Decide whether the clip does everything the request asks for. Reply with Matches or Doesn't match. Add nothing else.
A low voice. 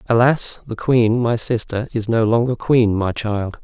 Matches